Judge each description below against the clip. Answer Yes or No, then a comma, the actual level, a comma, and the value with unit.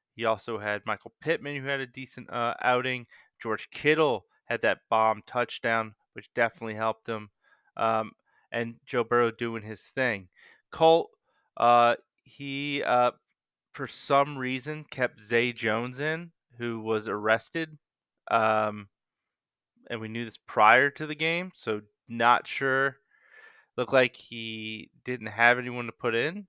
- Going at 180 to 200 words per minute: No, average, 145 wpm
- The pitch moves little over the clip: No, average, 3.8 semitones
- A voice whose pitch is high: No, low, 120 Hz